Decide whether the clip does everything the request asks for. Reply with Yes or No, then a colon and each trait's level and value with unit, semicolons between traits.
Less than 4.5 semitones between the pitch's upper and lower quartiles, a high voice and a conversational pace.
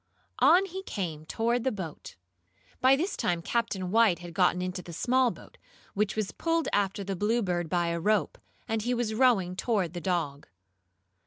No: average, 5.3 semitones; high, 200 Hz; average, 175 wpm